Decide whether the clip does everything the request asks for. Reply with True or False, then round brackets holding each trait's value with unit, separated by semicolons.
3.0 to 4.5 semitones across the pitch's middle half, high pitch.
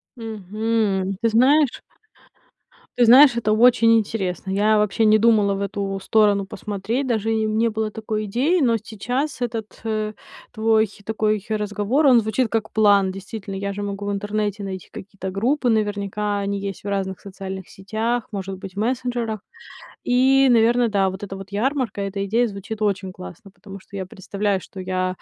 False (2.5 semitones; 210 Hz)